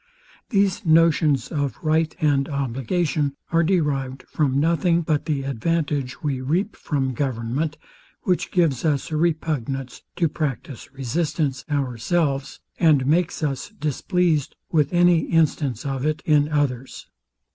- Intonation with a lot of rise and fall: No, average, 3.4 semitones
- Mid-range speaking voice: Yes, medium, 150 Hz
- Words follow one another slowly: Yes, slow, 125 wpm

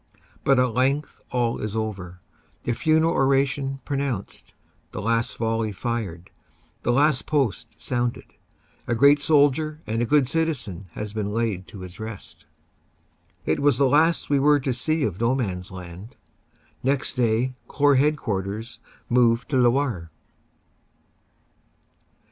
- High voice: No, low, 120 Hz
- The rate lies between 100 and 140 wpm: Yes, slow, 135 wpm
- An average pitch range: Yes, average, 4.6 semitones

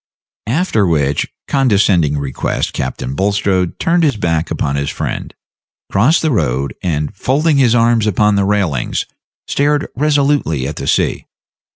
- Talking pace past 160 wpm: No, average, 140 wpm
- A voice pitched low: Yes, low, 100 Hz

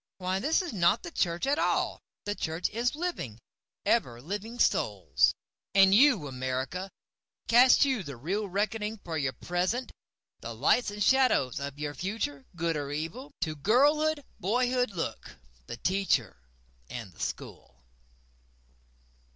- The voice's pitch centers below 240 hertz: Yes, high, 190 Hz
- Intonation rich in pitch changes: Yes, wide, 8.8 semitones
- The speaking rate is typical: No, slow, 120 wpm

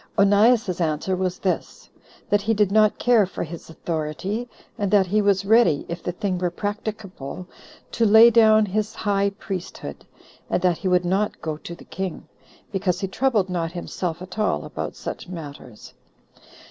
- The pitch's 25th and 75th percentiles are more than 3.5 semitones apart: No, average, 3.1 semitones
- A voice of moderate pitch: No, high, 195 Hz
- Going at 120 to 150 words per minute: No, average, 170 wpm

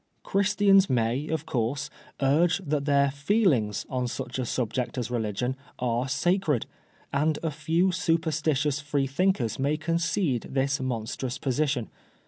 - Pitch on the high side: No, medium, 140 Hz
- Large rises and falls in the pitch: No, average, 4.3 semitones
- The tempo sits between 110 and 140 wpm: Yes, slow, 135 wpm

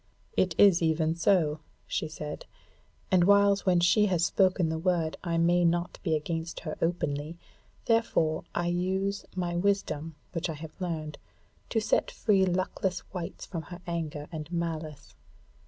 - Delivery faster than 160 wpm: No, average, 155 wpm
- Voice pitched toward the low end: No, medium, 170 Hz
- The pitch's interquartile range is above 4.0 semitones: No, narrow, 2.6 semitones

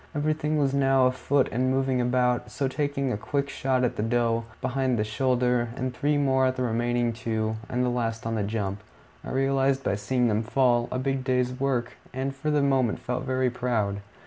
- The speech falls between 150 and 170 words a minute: No, average, 200 wpm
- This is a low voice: Yes, low, 125 Hz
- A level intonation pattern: Yes, narrow, 2.2 semitones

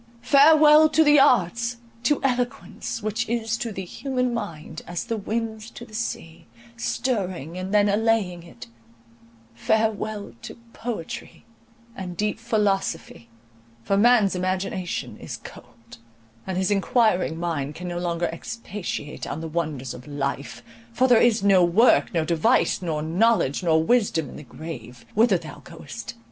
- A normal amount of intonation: No, wide, 6.2 semitones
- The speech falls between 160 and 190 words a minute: No, average, 140 wpm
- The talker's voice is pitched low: No, high, 190 Hz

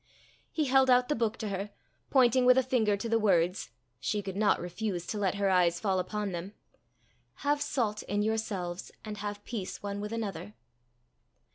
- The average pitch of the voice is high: Yes, high, 210 Hz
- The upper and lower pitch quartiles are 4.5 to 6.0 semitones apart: No, average, 3.1 semitones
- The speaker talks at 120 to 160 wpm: No, average, 180 wpm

